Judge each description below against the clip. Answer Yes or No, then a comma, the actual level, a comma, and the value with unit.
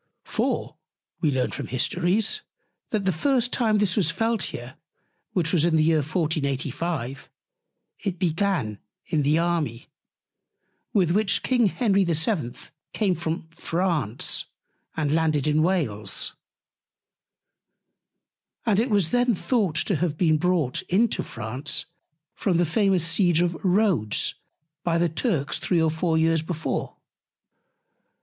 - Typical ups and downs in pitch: Yes, average, 4.0 semitones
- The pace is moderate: No, slow, 130 wpm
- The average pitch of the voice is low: No, medium, 170 Hz